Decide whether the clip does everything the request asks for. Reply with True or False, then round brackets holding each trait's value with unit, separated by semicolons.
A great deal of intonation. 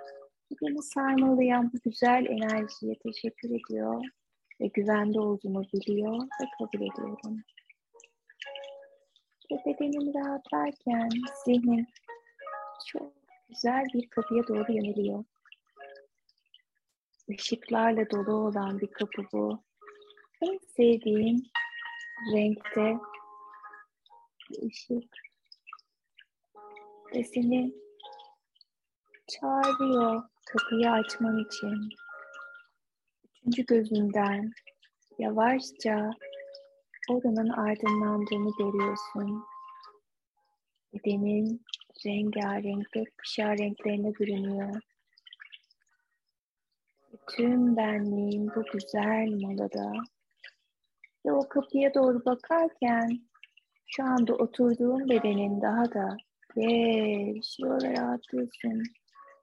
False (4.9 semitones)